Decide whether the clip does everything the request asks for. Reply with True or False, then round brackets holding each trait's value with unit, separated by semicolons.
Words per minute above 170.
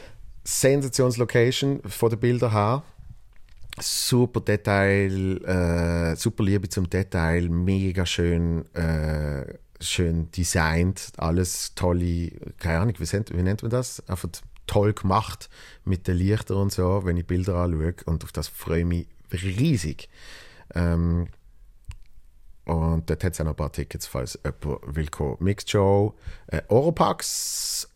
False (135 wpm)